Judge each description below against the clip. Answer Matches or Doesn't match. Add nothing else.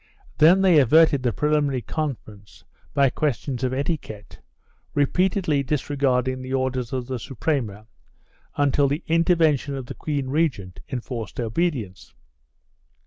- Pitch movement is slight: Doesn't match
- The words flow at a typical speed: Doesn't match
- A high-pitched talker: Doesn't match